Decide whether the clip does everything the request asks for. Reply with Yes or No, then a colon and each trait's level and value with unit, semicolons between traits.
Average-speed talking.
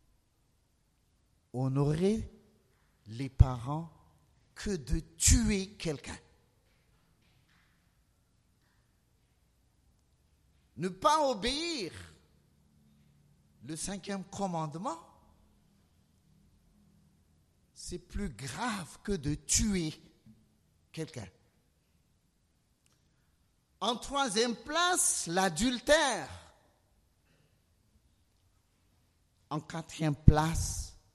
No: slow, 50 wpm